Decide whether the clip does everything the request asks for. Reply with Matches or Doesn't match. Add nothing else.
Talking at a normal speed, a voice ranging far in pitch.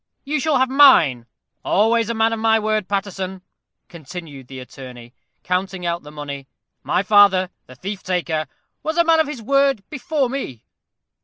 Matches